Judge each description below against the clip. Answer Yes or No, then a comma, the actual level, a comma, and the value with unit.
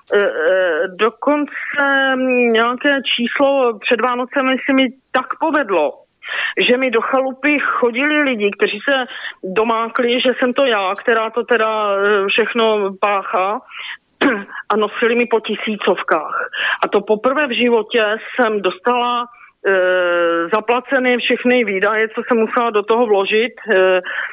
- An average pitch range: Yes, average, 3.5 semitones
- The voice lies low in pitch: No, high, 240 Hz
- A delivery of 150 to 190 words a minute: No, average, 125 wpm